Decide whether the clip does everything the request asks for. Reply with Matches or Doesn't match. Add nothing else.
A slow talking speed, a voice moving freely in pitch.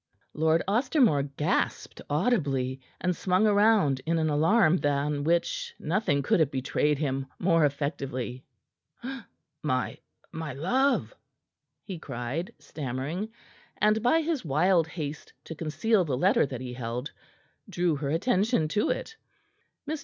Matches